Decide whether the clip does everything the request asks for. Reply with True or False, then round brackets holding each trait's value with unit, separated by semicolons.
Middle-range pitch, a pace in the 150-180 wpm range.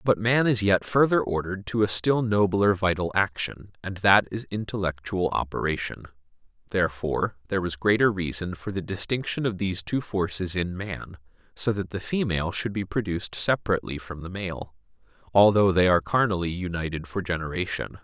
False (95 Hz; 165 wpm)